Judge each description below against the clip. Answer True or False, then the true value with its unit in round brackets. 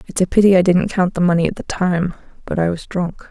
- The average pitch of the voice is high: False (180 Hz)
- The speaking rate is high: True (270 wpm)